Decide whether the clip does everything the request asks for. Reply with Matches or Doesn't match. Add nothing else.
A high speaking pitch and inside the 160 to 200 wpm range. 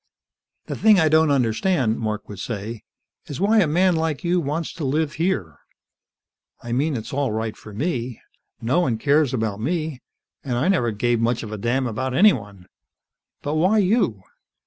Doesn't match